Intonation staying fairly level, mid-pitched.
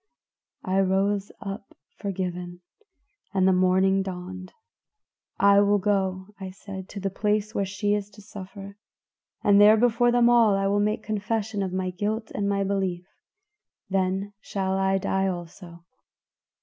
No: narrow, 1.5 semitones; high, 195 Hz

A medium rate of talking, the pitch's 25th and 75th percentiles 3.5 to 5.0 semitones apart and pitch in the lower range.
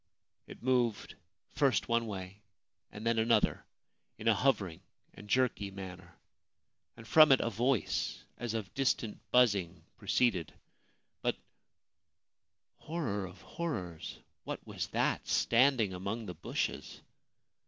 No: slow, 125 wpm; average, 4.5 semitones; low, 110 Hz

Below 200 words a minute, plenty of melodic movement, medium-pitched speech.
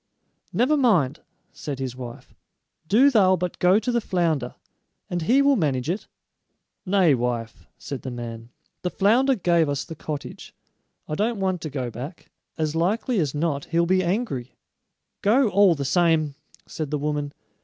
Yes: average, 165 wpm; wide, 6.2 semitones; medium, 165 Hz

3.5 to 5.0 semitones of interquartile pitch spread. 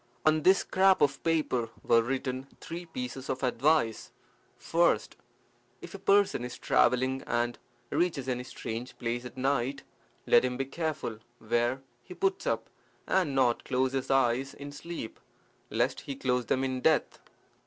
Yes: average, 4.0 semitones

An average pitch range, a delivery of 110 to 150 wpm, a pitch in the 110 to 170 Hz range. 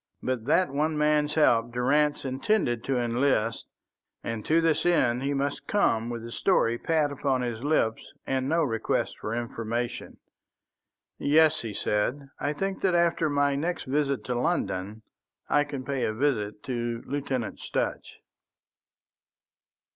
Yes: average, 4.2 semitones; average, 145 wpm; low, 135 Hz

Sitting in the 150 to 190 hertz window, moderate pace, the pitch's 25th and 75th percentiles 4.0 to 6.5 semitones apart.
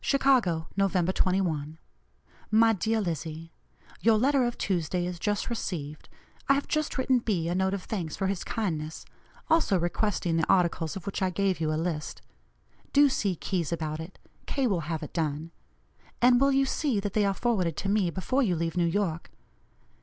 Yes: medium, 185 Hz; average, 185 wpm; average, 5.0 semitones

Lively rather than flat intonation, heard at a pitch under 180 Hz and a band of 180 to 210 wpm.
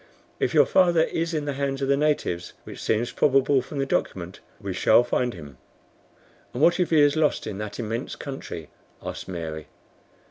Yes: wide, 7.1 semitones; low, 135 Hz; average, 185 wpm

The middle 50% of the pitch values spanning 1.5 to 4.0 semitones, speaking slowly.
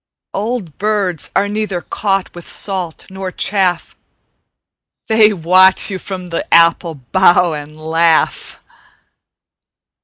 Yes: average, 2.8 semitones; slow, 110 wpm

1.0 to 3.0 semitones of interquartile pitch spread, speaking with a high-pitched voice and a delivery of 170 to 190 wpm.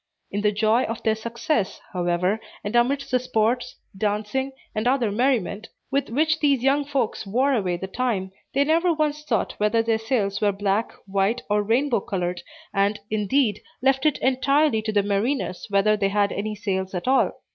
No: average, 4.6 semitones; high, 220 Hz; average, 180 wpm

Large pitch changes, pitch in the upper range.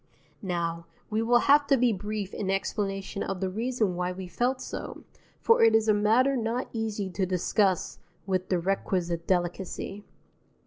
No: average, 3.6 semitones; high, 200 Hz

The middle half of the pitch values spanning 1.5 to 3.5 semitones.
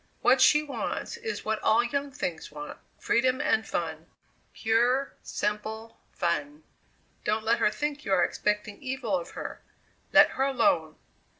No: average, 4.6 semitones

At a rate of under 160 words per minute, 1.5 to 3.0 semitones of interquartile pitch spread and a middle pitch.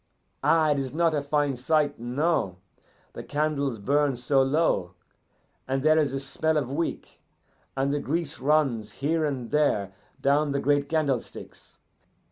Yes: average, 150 wpm; narrow, 2.4 semitones; medium, 145 Hz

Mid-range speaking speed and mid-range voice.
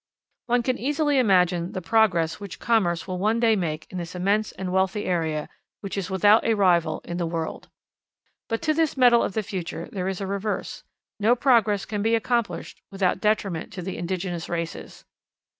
No: average, 185 wpm; high, 195 Hz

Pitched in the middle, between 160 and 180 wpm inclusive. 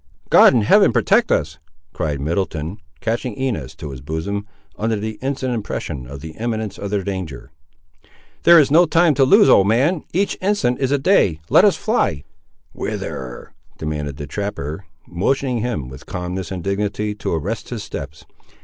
No: low, 100 Hz; average, 165 wpm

